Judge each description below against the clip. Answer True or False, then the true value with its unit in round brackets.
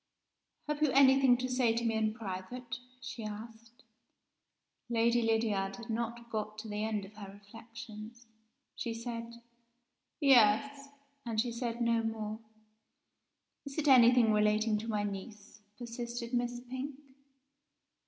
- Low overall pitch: False (230 Hz)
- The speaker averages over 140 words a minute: False (135 wpm)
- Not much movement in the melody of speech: True (2.1 semitones)